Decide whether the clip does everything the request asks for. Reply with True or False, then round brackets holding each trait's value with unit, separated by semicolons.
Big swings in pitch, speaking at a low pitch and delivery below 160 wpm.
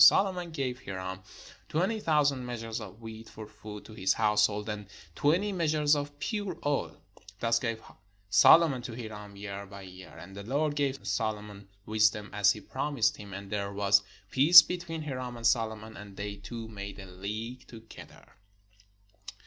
False (5.7 semitones; 110 Hz; 165 wpm)